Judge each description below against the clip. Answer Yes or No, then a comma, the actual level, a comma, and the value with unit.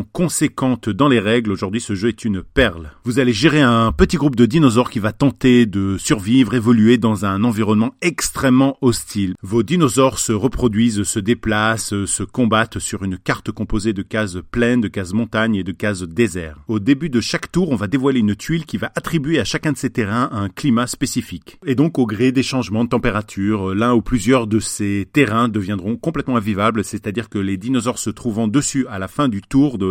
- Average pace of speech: Yes, average, 210 wpm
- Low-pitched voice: Yes, low, 115 Hz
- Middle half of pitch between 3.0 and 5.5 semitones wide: Yes, average, 3.9 semitones